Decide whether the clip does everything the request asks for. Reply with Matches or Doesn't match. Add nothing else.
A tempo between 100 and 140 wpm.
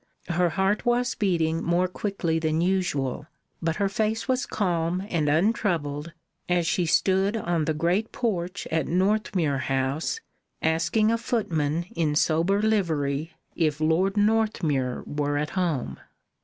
Matches